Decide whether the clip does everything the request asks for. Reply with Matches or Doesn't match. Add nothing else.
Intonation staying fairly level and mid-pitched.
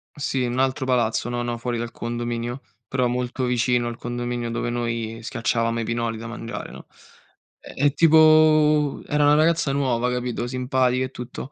Doesn't match